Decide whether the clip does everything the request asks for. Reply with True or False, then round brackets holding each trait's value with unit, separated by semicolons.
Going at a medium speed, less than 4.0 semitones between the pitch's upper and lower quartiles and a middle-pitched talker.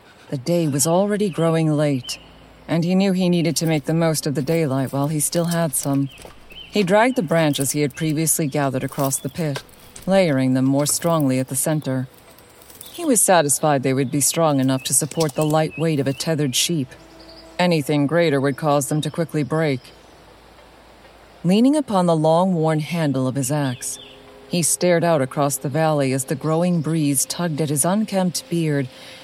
True (185 wpm; 3.2 semitones; 155 Hz)